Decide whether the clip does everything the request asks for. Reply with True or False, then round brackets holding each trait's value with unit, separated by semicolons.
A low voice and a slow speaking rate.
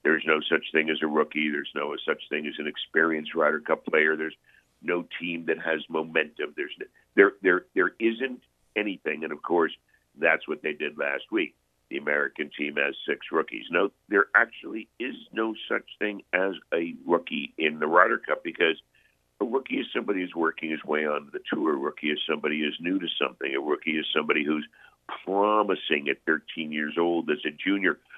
False (80 Hz; 200 wpm)